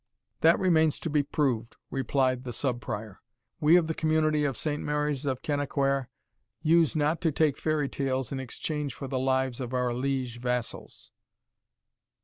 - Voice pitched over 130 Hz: Yes, medium, 140 Hz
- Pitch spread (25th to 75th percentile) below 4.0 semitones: Yes, average, 3.0 semitones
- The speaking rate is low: No, average, 160 wpm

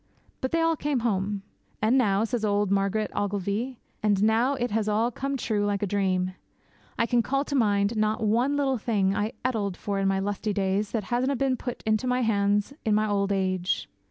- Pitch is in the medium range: No, high, 215 Hz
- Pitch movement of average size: Yes, average, 3.4 semitones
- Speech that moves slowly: No, fast, 205 wpm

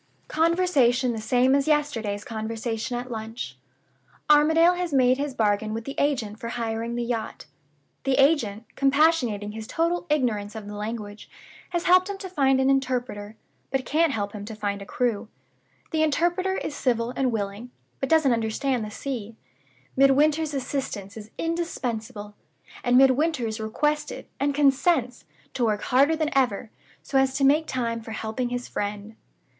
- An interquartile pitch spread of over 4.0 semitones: Yes, average, 4.8 semitones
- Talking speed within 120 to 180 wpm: Yes, average, 160 wpm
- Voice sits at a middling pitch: No, very high, 250 Hz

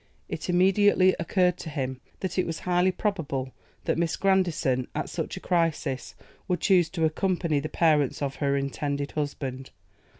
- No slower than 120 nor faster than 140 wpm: No, average, 160 wpm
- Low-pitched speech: No, medium, 165 Hz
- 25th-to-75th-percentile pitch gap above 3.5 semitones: Yes, average, 4.4 semitones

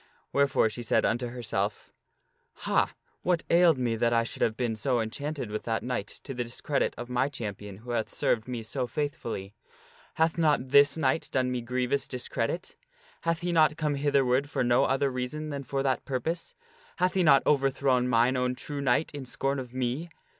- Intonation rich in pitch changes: No, average, 3.1 semitones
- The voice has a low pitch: Yes, low, 130 Hz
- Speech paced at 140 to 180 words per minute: No, average, 190 wpm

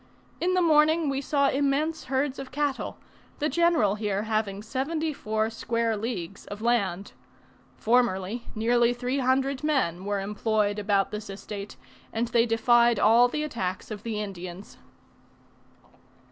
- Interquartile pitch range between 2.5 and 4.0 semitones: No, average, 4.8 semitones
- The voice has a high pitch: Yes, high, 230 Hz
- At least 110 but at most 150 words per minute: Yes, average, 140 wpm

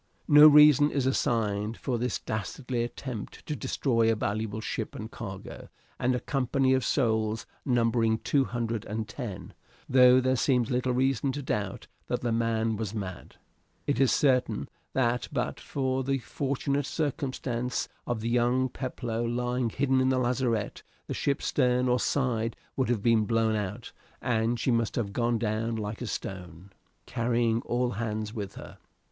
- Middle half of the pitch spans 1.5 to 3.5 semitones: Yes, average, 2.7 semitones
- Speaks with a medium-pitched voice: No, low, 120 Hz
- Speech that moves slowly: No, average, 160 wpm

